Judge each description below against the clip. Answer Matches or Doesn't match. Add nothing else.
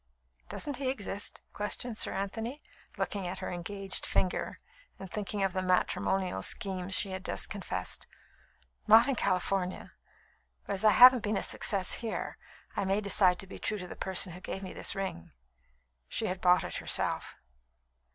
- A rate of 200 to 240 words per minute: Doesn't match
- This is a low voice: Doesn't match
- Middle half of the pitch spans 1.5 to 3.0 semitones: Matches